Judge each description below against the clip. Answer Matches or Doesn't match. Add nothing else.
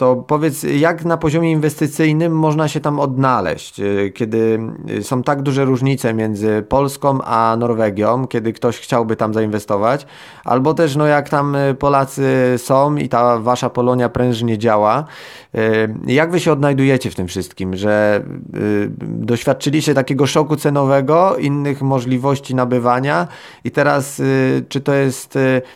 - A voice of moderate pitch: Doesn't match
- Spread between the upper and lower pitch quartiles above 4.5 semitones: Doesn't match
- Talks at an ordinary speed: Matches